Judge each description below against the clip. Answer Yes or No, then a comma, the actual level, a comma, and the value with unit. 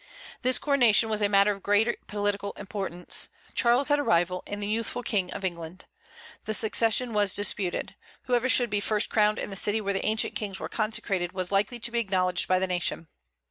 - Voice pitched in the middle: No, high, 205 Hz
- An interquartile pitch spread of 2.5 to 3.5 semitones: Yes, average, 2.9 semitones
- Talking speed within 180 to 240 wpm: Yes, average, 200 wpm